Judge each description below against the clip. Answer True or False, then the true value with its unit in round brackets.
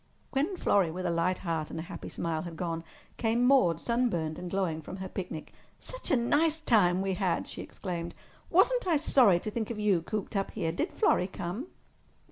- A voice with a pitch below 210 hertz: True (190 Hz)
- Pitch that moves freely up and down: True (5.9 semitones)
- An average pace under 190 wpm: False (205 wpm)